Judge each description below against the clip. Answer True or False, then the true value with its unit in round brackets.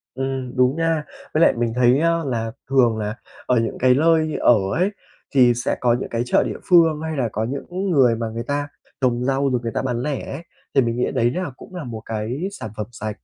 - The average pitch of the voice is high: False (130 Hz)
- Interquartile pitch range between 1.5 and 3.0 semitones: False (4.2 semitones)